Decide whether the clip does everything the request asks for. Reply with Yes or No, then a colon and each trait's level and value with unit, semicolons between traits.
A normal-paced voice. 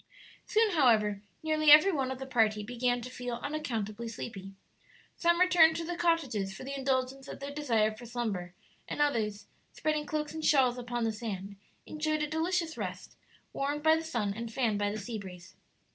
Yes: average, 185 wpm